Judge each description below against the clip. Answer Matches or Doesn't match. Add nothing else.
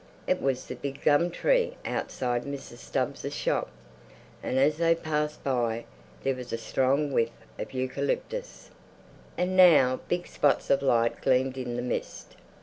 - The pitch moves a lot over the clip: Doesn't match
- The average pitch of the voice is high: Doesn't match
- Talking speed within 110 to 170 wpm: Matches